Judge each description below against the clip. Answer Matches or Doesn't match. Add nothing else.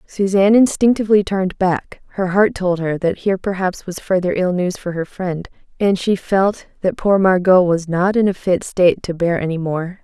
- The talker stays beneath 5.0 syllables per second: Doesn't match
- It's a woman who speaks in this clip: Matches